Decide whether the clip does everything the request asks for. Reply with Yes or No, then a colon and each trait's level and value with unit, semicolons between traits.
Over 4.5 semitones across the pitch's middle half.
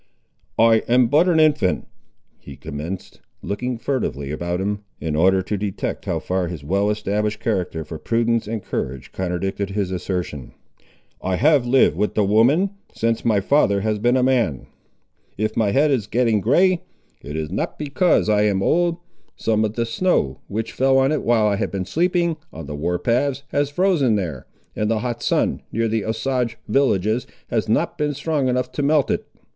Yes: wide, 5.6 semitones